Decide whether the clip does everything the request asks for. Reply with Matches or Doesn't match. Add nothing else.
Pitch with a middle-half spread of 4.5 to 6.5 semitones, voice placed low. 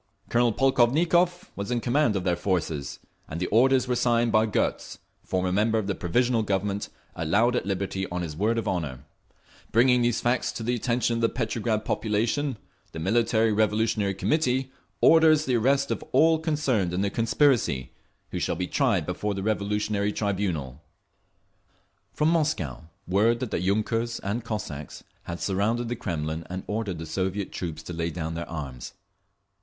Matches